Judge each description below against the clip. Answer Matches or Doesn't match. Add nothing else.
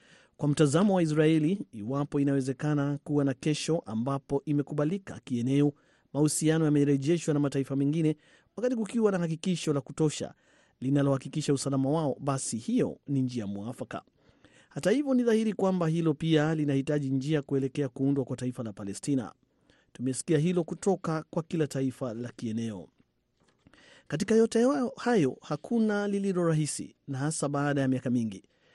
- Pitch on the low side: Doesn't match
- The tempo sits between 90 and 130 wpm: Doesn't match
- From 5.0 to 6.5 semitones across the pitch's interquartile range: Doesn't match